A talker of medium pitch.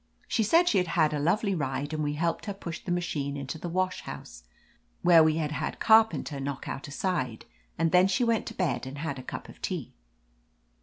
Yes: medium, 165 Hz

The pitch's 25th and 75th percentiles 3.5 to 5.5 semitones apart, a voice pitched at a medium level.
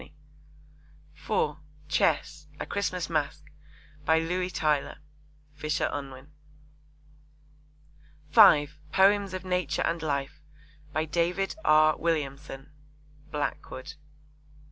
No: average, 2.8 semitones; medium, 155 Hz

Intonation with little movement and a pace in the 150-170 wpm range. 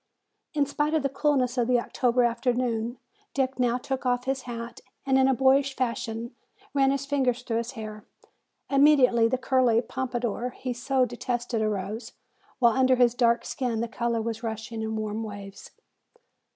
Yes: narrow, 2.3 semitones; average, 165 wpm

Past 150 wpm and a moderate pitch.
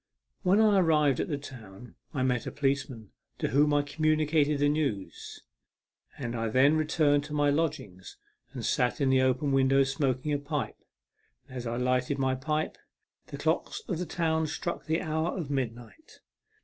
Yes: average, 175 wpm; medium, 145 Hz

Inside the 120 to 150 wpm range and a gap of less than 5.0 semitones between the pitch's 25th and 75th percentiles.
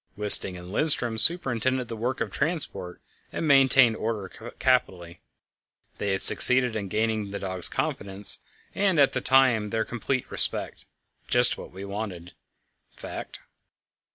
Yes: average, 145 wpm; average, 4.6 semitones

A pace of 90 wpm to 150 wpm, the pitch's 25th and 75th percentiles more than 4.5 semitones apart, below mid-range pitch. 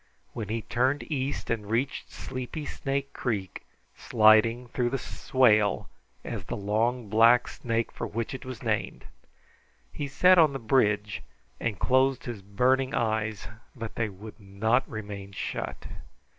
No: average, 145 wpm; average, 3.4 semitones; low, 115 Hz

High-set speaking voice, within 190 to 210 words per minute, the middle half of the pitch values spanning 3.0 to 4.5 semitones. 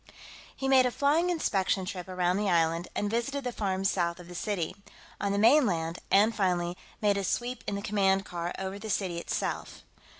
Yes: high, 195 Hz; average, 195 wpm; average, 3.8 semitones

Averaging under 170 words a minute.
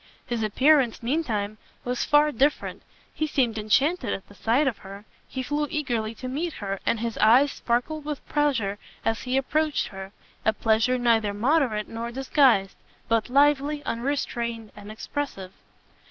Yes: average, 155 wpm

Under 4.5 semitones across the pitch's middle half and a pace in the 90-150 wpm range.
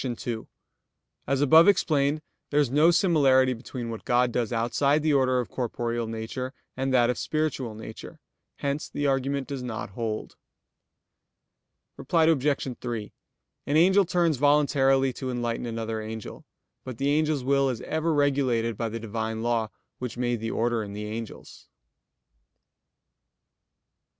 Yes: average, 3.8 semitones; average, 145 wpm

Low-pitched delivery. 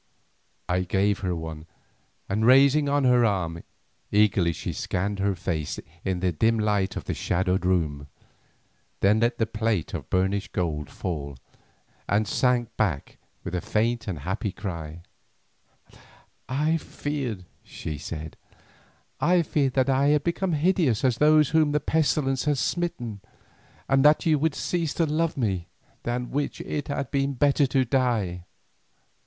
Yes: low, 115 Hz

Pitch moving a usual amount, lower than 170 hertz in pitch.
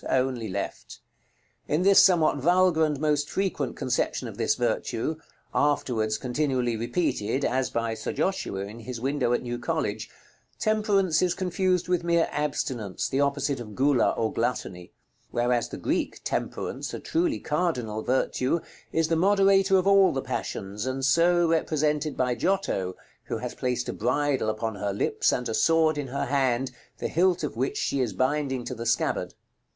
No: wide, 5.8 semitones; medium, 140 Hz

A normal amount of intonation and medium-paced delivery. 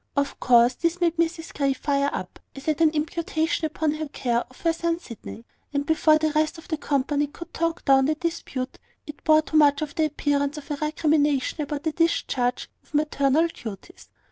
No: narrow, 2.3 semitones; average, 195 wpm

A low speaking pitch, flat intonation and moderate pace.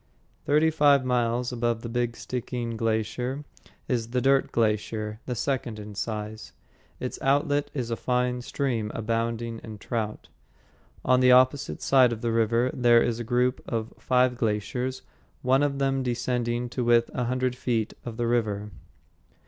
Yes: low, 120 Hz; narrow, 2.0 semitones; average, 155 wpm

